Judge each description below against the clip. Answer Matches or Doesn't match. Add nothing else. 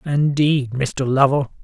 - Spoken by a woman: Doesn't match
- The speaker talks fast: Doesn't match